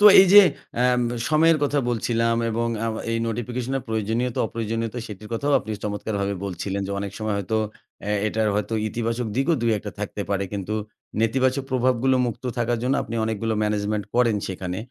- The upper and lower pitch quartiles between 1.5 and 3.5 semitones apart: Yes, average, 2.9 semitones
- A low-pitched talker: Yes, low, 115 Hz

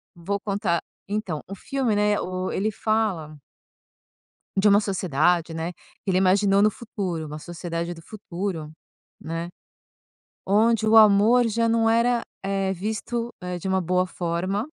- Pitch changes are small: No, average, 3.7 semitones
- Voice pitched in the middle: No, high, 195 Hz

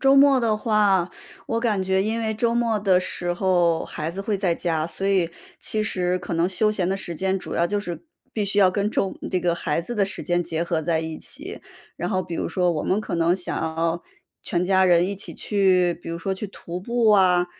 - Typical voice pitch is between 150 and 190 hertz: Yes, medium, 185 Hz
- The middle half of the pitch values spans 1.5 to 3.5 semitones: Yes, average, 3.1 semitones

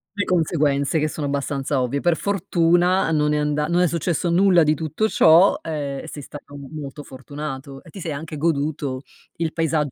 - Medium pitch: Yes, medium, 155 Hz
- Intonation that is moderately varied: Yes, average, 3.0 semitones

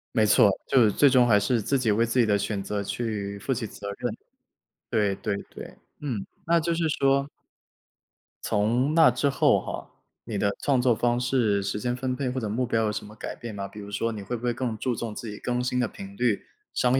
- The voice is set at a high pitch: No, low, 120 Hz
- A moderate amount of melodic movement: Yes, average, 3.4 semitones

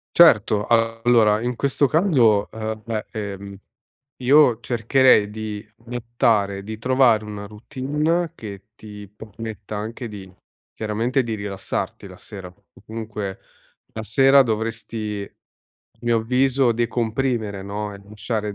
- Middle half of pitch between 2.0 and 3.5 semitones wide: Yes, narrow, 2.6 semitones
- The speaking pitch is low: Yes, low, 110 Hz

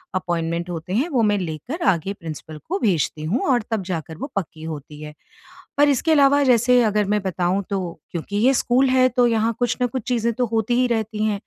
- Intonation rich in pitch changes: Yes, wide, 6.3 semitones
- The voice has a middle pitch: No, high, 210 Hz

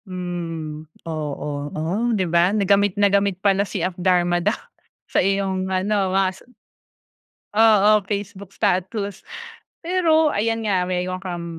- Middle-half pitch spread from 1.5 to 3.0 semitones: Yes, narrow, 2.4 semitones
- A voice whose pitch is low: No, high, 190 Hz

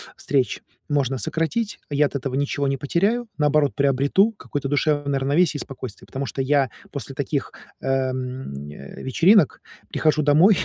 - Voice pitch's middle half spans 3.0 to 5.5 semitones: No, narrow, 2.5 semitones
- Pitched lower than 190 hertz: Yes, medium, 140 Hz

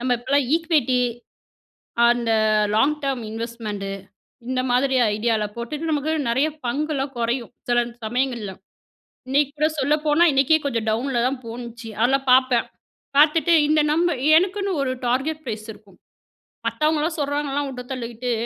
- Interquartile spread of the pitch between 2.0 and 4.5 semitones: Yes, average, 4.0 semitones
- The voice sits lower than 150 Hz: No, very high, 265 Hz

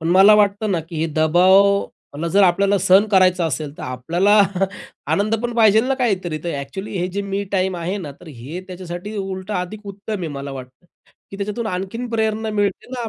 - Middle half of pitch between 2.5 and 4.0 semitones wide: Yes, average, 3.1 semitones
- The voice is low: No, high, 190 Hz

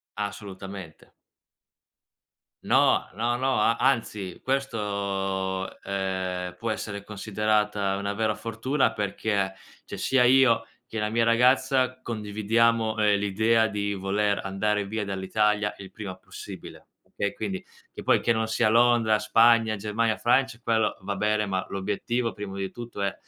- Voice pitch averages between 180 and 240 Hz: No, low, 105 Hz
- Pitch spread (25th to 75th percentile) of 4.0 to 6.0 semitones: No, narrow, 2.5 semitones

